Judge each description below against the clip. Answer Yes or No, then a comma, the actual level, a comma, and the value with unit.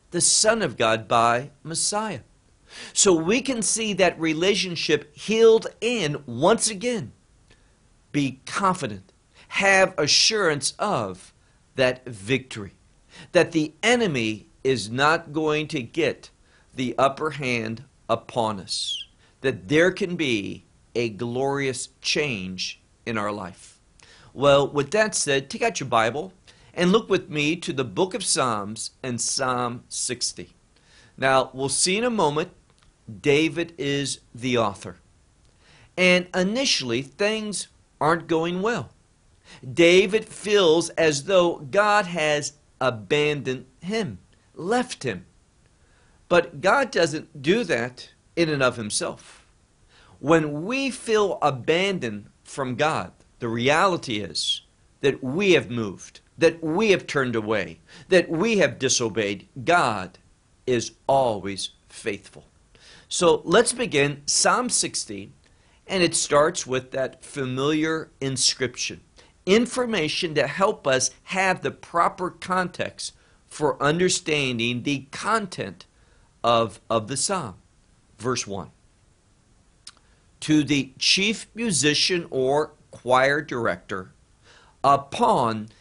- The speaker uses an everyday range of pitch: No, wide, 7.0 semitones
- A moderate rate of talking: No, slow, 115 wpm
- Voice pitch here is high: No, medium, 140 Hz